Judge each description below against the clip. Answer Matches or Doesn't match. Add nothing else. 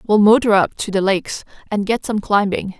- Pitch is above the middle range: Matches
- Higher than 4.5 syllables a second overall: Matches